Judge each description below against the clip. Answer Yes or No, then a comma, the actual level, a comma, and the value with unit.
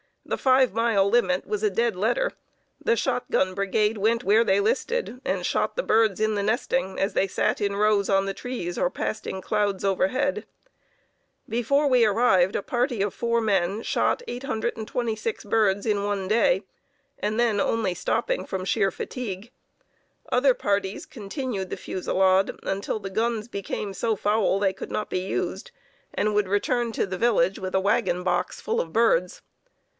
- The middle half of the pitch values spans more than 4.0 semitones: No, average, 3.4 semitones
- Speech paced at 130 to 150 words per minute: No, average, 170 wpm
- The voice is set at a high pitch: Yes, high, 210 Hz